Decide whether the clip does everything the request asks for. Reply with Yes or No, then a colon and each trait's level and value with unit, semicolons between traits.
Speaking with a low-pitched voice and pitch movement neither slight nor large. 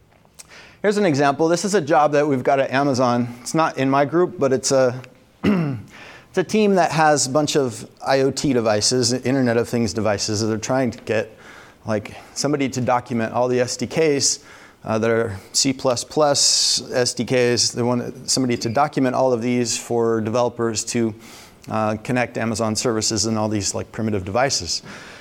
Yes: low, 125 Hz; average, 3.5 semitones